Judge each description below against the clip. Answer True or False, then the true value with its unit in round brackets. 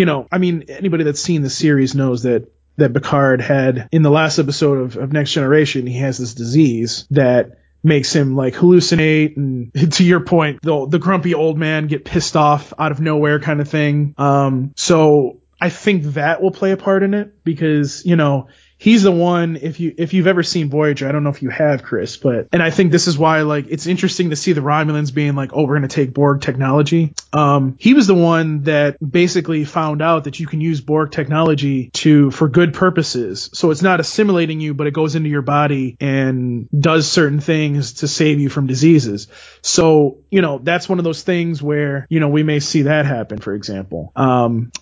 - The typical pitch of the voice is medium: True (150 Hz)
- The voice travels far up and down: False (2.8 semitones)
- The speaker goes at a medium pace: False (215 wpm)